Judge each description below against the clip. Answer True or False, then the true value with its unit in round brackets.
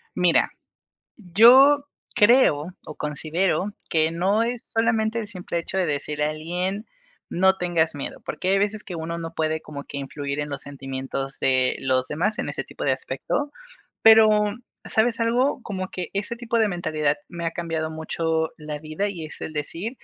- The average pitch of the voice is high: False (170 Hz)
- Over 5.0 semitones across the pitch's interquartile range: True (5.4 semitones)